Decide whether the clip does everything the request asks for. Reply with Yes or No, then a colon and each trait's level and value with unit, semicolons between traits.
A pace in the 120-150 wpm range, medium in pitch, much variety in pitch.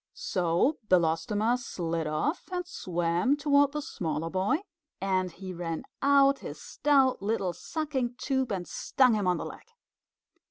No: average, 145 wpm; high, 205 Hz; wide, 8.0 semitones